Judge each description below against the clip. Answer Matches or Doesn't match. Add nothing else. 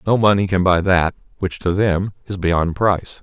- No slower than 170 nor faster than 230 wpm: Matches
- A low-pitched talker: Matches